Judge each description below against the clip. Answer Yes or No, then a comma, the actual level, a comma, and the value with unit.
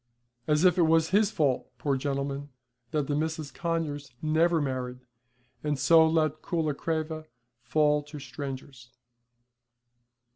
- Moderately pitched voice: Yes, medium, 150 Hz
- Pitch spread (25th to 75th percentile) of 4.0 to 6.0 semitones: No, narrow, 2.4 semitones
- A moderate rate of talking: No, slow, 120 wpm